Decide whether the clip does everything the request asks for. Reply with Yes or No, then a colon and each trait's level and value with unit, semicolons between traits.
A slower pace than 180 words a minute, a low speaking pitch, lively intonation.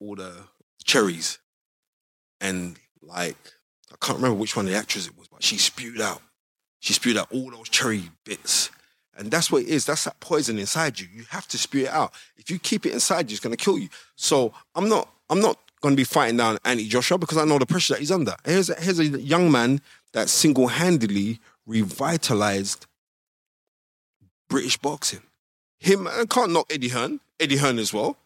No: average, 200 wpm; low, 130 Hz; wide, 6.9 semitones